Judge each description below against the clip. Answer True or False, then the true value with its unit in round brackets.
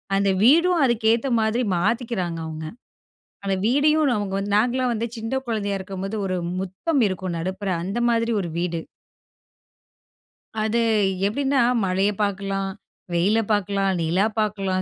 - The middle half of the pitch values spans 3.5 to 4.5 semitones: True (3.8 semitones)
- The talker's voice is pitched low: False (205 Hz)